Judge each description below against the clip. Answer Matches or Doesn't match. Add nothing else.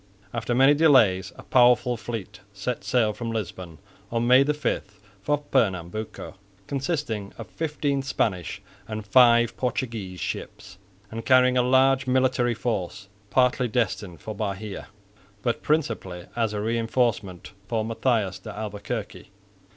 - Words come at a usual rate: Doesn't match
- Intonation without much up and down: Doesn't match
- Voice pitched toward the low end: Matches